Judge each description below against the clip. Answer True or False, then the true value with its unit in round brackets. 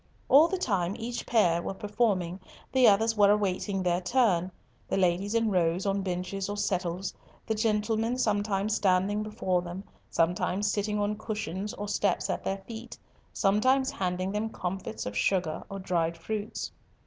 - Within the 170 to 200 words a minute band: False (160 wpm)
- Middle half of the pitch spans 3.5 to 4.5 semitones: False (2.8 semitones)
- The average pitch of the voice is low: False (200 Hz)